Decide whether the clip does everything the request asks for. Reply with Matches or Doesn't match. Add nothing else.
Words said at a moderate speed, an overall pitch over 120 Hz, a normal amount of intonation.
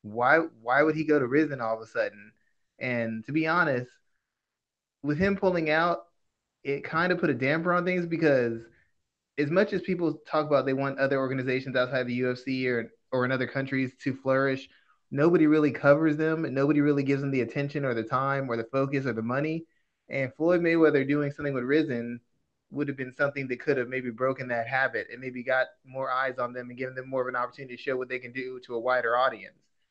Doesn't match